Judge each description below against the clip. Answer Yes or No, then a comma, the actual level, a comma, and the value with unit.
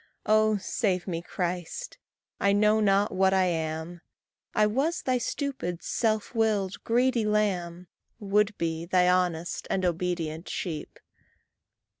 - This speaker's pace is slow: Yes, slow, 125 wpm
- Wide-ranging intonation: No, average, 3.6 semitones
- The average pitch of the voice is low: No, high, 190 Hz